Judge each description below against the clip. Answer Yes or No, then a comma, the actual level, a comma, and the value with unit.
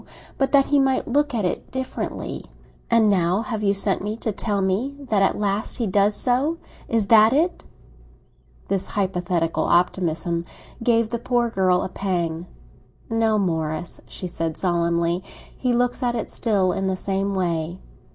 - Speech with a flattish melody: No, average, 4.5 semitones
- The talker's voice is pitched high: Yes, high, 200 Hz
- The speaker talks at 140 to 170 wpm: Yes, average, 165 wpm